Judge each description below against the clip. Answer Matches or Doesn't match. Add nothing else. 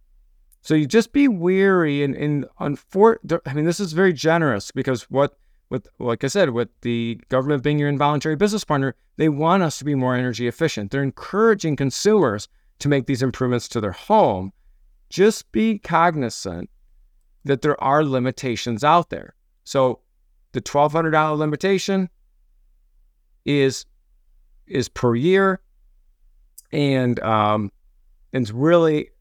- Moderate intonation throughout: Doesn't match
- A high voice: Doesn't match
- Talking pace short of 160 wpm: Matches